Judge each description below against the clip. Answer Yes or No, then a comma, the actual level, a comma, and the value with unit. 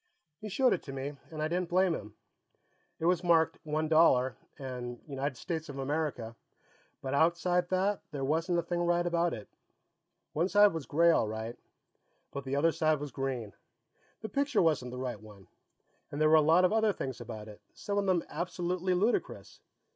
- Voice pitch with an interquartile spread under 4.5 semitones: No, average, 4.8 semitones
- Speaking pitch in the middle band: Yes, medium, 160 Hz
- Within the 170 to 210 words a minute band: Yes, average, 190 wpm